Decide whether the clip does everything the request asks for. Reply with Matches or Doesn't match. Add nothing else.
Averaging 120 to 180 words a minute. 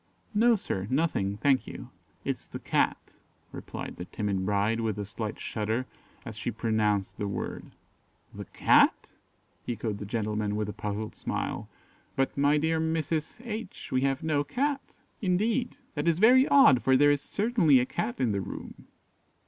Matches